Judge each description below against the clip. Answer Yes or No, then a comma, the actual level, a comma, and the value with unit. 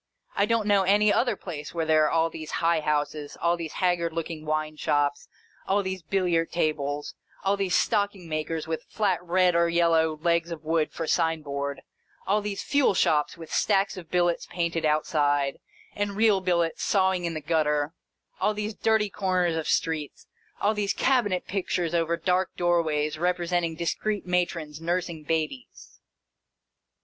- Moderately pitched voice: Yes, medium, 170 Hz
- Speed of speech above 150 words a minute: Yes, average, 160 wpm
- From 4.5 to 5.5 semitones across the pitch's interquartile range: No, average, 3.2 semitones